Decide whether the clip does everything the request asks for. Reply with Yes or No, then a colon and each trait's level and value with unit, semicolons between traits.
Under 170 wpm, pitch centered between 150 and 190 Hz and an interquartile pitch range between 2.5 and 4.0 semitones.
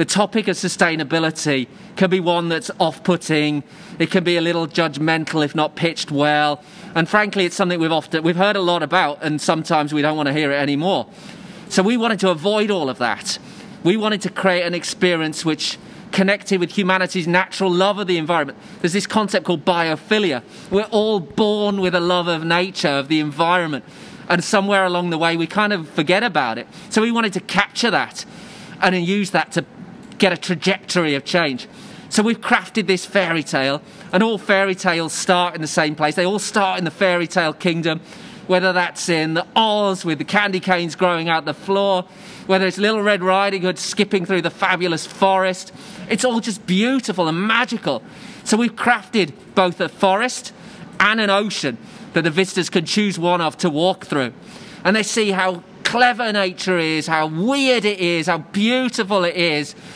No: average, 190 wpm; medium, 185 Hz; average, 3.4 semitones